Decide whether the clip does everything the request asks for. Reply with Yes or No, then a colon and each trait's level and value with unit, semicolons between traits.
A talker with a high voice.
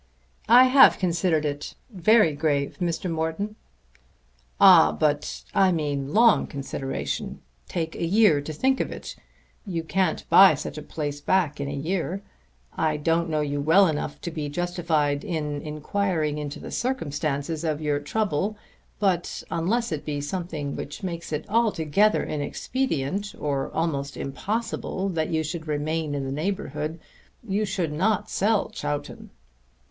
No: medium, 160 Hz